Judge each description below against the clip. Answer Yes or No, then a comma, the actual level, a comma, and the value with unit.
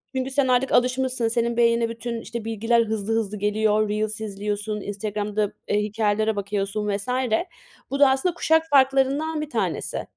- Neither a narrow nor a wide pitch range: Yes, average, 3.7 semitones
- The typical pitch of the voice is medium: No, high, 225 Hz